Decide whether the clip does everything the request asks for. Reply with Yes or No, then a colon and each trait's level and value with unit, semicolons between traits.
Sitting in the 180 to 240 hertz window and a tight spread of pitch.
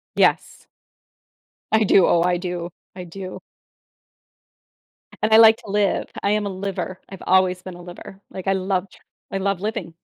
Yes: high, 190 Hz; narrow, 1.8 semitones